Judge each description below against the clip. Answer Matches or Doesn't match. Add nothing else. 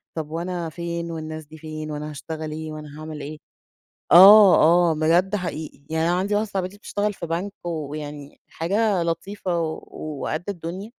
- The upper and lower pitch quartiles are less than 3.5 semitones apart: Matches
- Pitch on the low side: Doesn't match